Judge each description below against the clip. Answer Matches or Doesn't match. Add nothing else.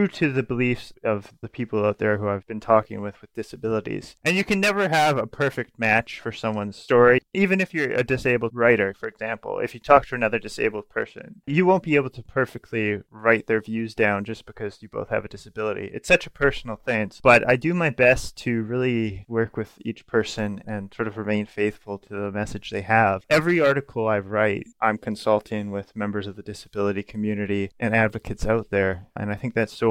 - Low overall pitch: Matches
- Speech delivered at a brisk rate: Matches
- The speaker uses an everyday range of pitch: Matches